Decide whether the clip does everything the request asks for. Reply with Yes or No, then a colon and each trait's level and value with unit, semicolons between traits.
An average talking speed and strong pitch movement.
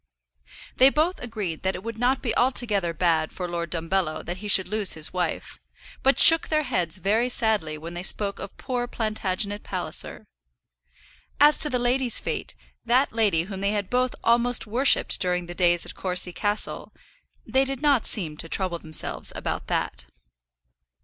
Yes: average, 170 wpm; wide, 5.8 semitones